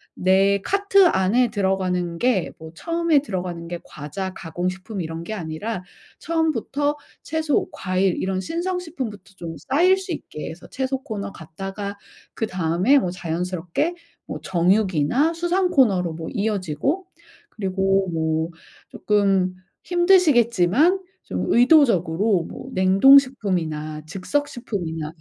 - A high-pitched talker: Yes, high, 195 Hz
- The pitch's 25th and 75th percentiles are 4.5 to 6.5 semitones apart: No, wide, 7.7 semitones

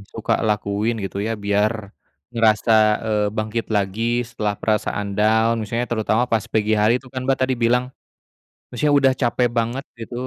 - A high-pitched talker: No, low, 115 Hz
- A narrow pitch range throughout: Yes, narrow, 2.2 semitones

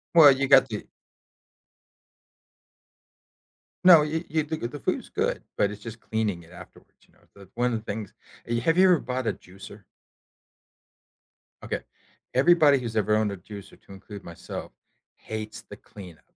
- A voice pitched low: Yes, low, 110 Hz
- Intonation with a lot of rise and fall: Yes, wide, 5.7 semitones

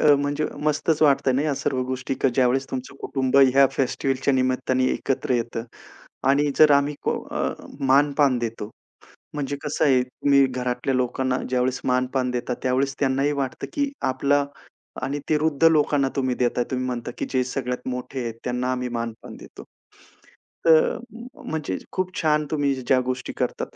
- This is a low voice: Yes, low, 130 Hz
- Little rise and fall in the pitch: Yes, narrow, 2.1 semitones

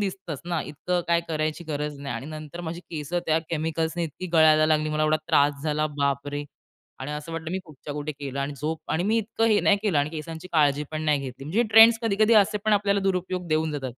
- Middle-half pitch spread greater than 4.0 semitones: No, average, 3.3 semitones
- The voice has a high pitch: No, medium, 155 Hz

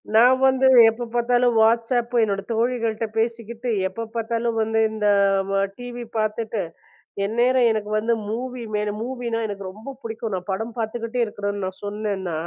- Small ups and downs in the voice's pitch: Yes, narrow, 2.0 semitones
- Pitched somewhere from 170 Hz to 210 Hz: No, high, 230 Hz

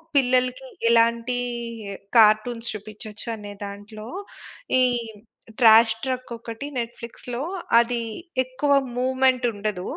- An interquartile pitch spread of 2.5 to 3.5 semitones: Yes, average, 2.8 semitones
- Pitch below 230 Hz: No, high, 235 Hz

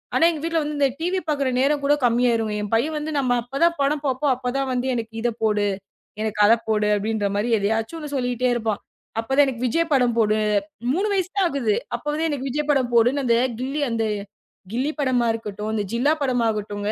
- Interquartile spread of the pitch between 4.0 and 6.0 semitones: Yes, average, 4.5 semitones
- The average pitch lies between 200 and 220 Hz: No, very high, 250 Hz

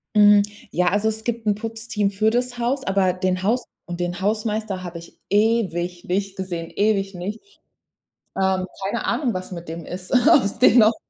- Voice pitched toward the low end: No, high, 205 Hz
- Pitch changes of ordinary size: Yes, average, 3.5 semitones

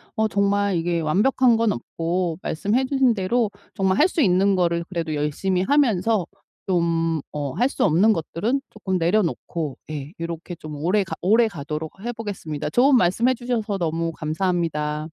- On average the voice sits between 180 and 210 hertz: Yes, medium, 185 Hz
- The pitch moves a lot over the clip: No, average, 5.0 semitones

